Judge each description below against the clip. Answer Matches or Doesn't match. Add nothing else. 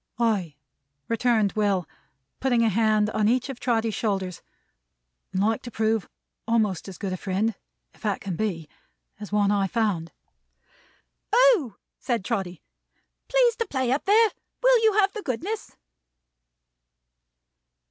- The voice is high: Matches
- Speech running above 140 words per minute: Doesn't match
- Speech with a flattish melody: Doesn't match